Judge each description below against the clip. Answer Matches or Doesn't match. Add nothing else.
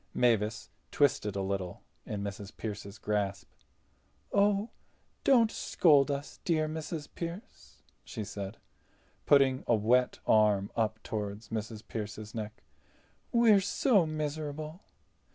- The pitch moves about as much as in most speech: Doesn't match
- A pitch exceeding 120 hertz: Doesn't match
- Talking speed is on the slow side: Matches